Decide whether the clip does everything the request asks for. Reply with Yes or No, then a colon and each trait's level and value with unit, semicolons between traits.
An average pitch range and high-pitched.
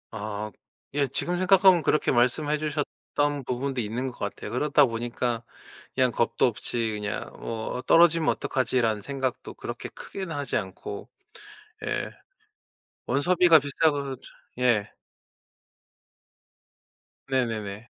No: average, 4.3 semitones; low, 130 Hz